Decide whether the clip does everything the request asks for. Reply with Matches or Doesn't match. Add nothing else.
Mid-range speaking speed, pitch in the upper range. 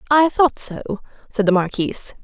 Matches